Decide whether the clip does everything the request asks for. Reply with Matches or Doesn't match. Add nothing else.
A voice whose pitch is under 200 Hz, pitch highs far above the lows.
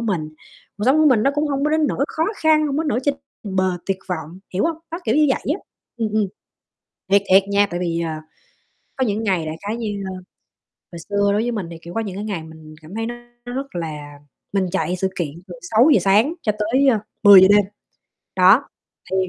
Doesn't match